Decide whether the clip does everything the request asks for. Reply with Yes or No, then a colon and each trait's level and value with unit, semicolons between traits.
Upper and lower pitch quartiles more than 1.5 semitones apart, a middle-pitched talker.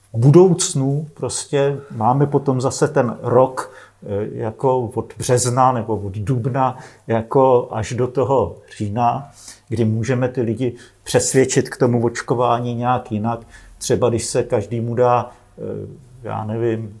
No: narrow, 2.5 semitones; low, 125 Hz